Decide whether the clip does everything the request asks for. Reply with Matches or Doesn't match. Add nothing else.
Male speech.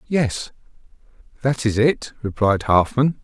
Matches